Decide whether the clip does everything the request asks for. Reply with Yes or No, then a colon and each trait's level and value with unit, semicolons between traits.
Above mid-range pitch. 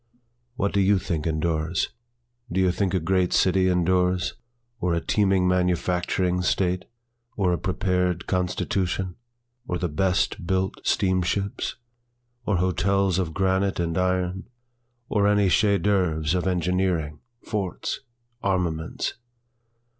No: very low, 90 Hz